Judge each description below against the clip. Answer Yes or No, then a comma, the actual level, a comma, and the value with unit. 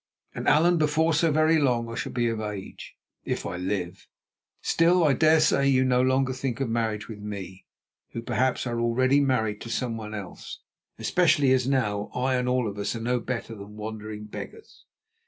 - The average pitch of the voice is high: No, low, 120 Hz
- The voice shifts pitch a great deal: No, average, 4.1 semitones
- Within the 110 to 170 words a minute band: No, average, 190 wpm